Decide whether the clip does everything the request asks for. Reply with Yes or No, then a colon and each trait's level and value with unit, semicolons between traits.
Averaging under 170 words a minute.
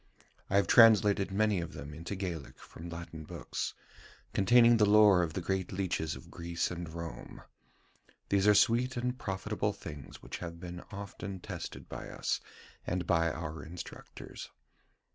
Yes: average, 155 wpm